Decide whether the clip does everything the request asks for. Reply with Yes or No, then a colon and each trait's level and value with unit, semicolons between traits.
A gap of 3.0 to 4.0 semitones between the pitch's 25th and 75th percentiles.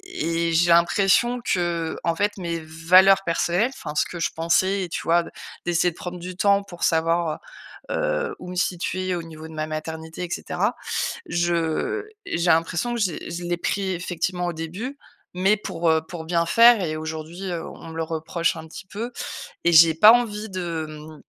No: narrow, 2.6 semitones